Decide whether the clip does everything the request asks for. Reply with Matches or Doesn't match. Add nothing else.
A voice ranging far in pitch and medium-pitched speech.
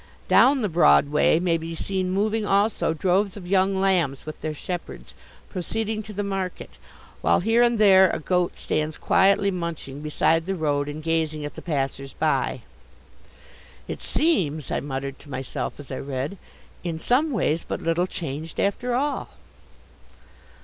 Doesn't match